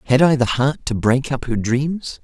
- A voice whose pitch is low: Yes, low, 130 Hz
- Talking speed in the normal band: No, fast, 240 wpm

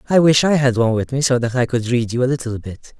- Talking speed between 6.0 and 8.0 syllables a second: Yes, 6.5 syllables/s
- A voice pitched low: Yes, low, 125 Hz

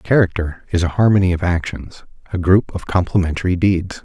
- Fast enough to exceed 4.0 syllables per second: Yes, 5.4 syllables/s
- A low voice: Yes, very low, 90 Hz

